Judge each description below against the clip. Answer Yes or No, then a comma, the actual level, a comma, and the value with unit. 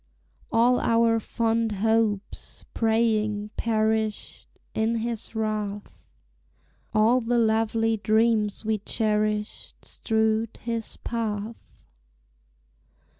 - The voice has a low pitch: No, high, 220 Hz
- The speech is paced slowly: Yes, slow, 80 wpm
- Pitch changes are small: Yes, narrow, 1.2 semitones